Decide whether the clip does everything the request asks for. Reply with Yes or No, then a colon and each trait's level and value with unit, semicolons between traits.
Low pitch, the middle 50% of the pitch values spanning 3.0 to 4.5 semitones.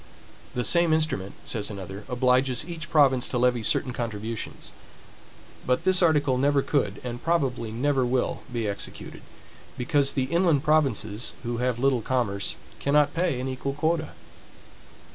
Yes: low, 130 Hz; average, 3.8 semitones